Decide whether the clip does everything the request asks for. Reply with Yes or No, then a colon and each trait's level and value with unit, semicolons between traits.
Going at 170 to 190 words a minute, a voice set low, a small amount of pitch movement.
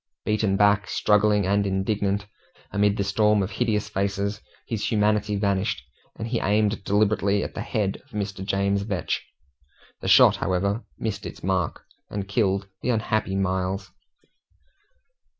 No: average, 140 wpm; low, 100 Hz; narrow, 1.4 semitones